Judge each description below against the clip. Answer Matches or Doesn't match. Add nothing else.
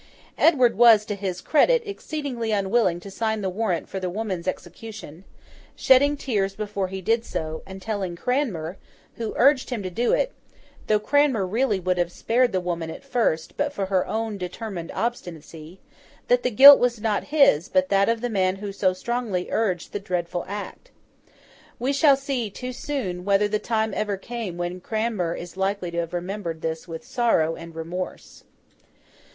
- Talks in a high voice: Matches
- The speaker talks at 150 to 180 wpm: Matches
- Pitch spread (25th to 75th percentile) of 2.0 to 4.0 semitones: Doesn't match